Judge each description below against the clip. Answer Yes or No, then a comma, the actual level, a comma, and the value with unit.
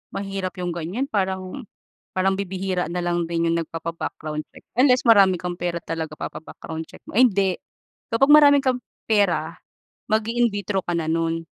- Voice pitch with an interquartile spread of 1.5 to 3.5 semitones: No, average, 4.0 semitones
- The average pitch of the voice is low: No, medium, 185 Hz